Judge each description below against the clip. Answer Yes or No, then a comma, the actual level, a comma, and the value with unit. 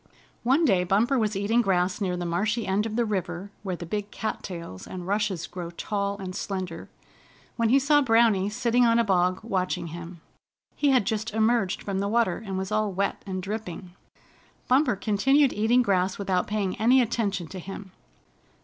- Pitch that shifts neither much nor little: Yes, average, 3.5 semitones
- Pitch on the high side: Yes, high, 200 Hz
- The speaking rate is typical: Yes, average, 180 wpm